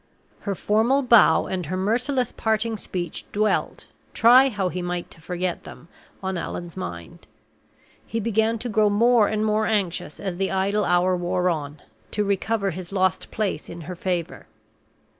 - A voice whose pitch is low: No, high, 195 Hz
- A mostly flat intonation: No, average, 3.7 semitones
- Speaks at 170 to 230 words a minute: No, average, 160 wpm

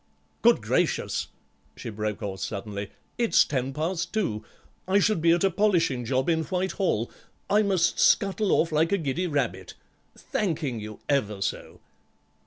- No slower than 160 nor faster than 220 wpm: No, average, 150 wpm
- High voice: No, medium, 155 Hz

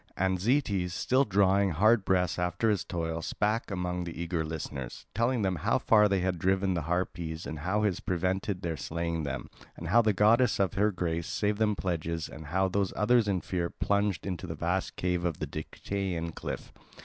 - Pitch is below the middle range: Yes, very low, 90 Hz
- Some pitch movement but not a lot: Yes, average, 3.2 semitones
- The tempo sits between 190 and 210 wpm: Yes, average, 195 wpm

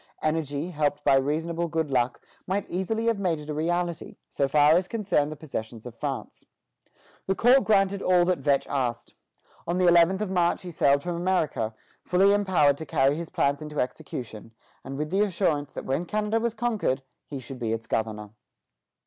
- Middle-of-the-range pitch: Yes, medium, 160 Hz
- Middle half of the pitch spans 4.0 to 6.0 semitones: Yes, average, 5.1 semitones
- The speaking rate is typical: Yes, average, 185 wpm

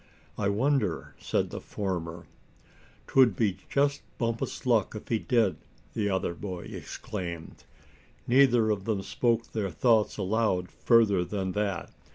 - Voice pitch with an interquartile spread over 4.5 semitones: No, average, 3.7 semitones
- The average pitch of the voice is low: Yes, low, 105 Hz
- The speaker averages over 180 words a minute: No, slow, 135 wpm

